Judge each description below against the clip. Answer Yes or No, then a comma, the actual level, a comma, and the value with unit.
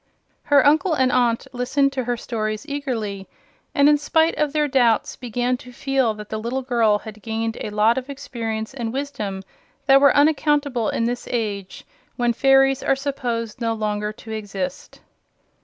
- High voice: Yes, high, 245 Hz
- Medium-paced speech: Yes, average, 170 wpm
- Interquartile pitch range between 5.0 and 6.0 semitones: No, average, 3.9 semitones